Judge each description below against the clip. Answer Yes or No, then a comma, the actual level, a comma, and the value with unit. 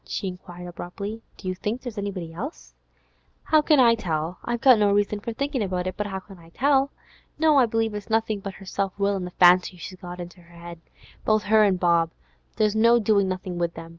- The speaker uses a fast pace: Yes, fast, 225 wpm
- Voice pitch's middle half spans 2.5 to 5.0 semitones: Yes, average, 3.8 semitones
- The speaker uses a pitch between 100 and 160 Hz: No, high, 200 Hz